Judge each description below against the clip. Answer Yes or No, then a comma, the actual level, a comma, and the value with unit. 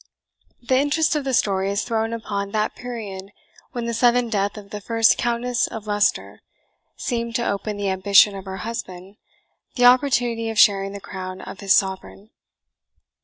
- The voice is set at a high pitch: Yes, high, 215 Hz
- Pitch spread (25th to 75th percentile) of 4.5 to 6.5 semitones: No, average, 3.2 semitones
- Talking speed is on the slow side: No, average, 170 wpm